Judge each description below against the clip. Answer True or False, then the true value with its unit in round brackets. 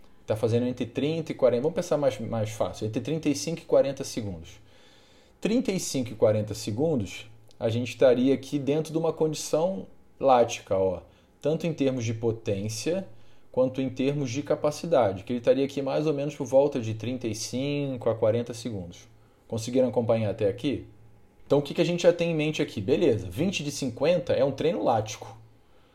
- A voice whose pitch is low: True (130 Hz)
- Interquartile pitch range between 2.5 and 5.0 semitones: True (4.7 semitones)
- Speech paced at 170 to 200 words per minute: True (180 wpm)